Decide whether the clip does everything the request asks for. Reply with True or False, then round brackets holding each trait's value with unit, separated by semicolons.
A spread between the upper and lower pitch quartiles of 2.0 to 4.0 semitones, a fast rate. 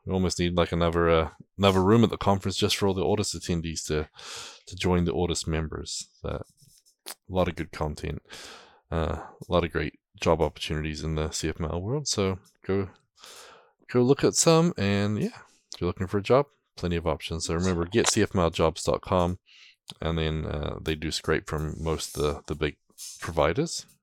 False (3.7 semitones; 185 wpm)